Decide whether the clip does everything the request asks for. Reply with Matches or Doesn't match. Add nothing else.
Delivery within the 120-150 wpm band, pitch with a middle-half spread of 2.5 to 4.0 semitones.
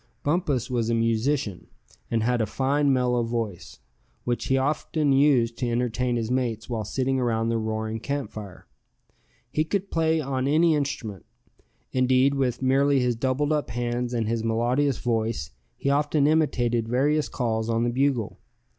Doesn't match